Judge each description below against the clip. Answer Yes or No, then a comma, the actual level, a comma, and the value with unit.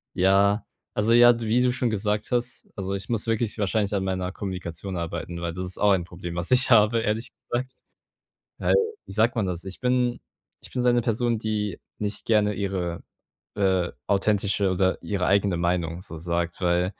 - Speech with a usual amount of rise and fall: Yes, average, 3.7 semitones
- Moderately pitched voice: No, low, 100 Hz